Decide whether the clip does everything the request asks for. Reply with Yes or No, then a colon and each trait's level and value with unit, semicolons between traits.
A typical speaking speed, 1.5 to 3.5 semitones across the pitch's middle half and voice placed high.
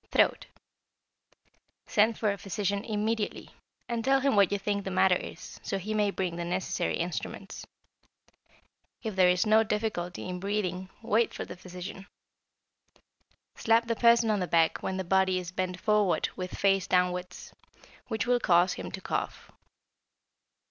Yes: average, 155 wpm; average, 3.1 semitones; high, 195 Hz